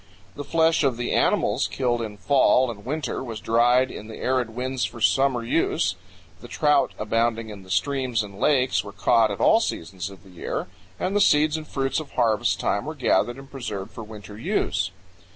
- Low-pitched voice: Yes, low, 120 Hz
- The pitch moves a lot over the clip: No, average, 4.1 semitones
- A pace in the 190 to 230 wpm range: Yes, average, 195 wpm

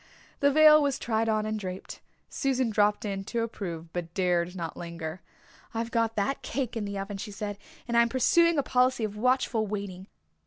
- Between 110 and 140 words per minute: No, average, 195 wpm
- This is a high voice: Yes, high, 215 Hz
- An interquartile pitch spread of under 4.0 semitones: No, average, 4.3 semitones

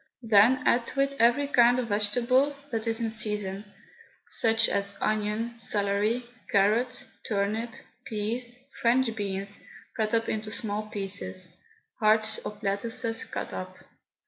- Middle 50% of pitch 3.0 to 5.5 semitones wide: No, narrow, 2.4 semitones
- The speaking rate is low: Yes, slow, 130 wpm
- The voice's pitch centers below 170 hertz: No, high, 220 Hz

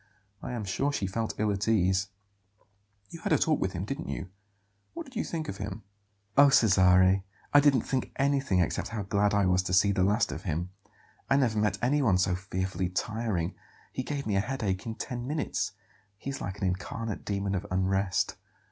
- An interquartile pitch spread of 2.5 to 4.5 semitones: No, average, 5.2 semitones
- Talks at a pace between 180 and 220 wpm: Yes, average, 200 wpm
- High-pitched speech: No, low, 100 Hz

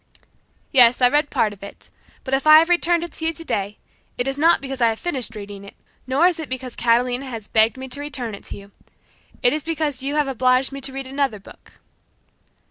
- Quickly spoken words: Yes, fast, 225 wpm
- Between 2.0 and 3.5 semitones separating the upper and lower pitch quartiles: No, average, 4.1 semitones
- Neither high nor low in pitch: No, very high, 265 Hz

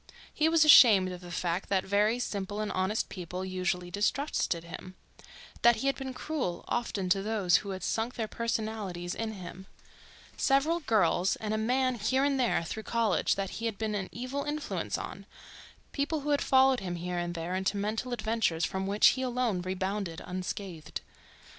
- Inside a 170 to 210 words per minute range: Yes, average, 180 wpm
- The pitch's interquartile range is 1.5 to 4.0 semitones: No, average, 4.9 semitones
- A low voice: No, high, 210 Hz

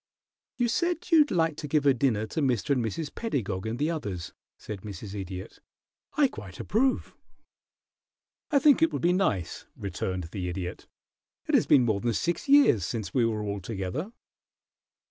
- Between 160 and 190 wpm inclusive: Yes, average, 170 wpm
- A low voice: Yes, low, 120 Hz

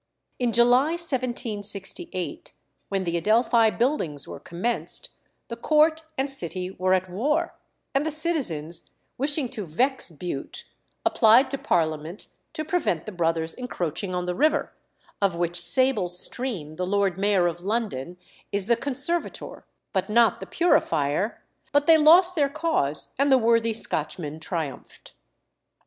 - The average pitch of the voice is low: No, high, 215 Hz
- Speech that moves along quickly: No, average, 140 wpm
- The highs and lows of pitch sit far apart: Yes, wide, 7.7 semitones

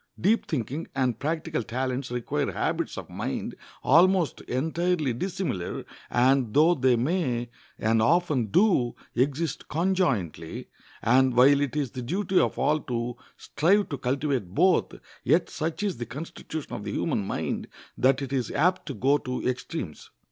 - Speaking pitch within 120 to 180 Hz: Yes, low, 135 Hz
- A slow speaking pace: No, average, 150 wpm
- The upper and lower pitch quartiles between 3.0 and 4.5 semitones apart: No, average, 5.2 semitones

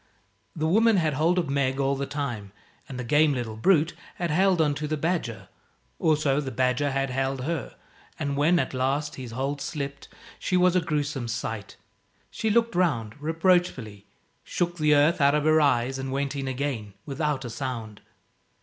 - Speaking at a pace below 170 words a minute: No, average, 180 wpm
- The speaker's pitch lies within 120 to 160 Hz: Yes, medium, 140 Hz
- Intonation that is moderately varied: Yes, average, 3.4 semitones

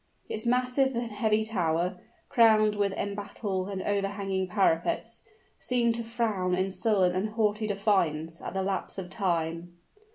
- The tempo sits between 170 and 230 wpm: No, average, 140 wpm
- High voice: Yes, high, 200 Hz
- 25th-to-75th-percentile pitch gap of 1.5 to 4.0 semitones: Yes, average, 3.1 semitones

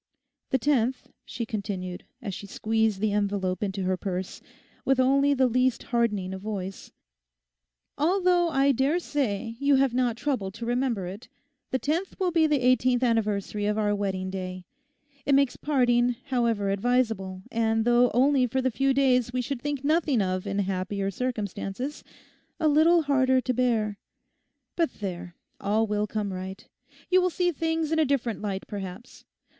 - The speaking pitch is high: Yes, high, 235 Hz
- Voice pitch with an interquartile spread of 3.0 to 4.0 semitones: No, average, 5.3 semitones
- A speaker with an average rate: Yes, average, 160 wpm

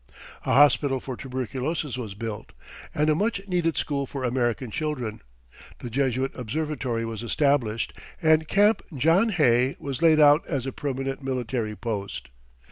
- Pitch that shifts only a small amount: No, average, 4.1 semitones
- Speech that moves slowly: No, average, 145 wpm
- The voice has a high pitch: No, low, 135 Hz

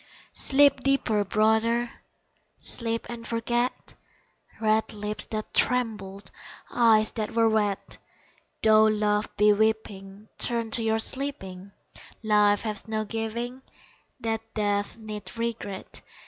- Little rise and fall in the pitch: Yes, narrow, 1.8 semitones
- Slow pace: Yes, slow, 110 wpm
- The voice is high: Yes, high, 220 Hz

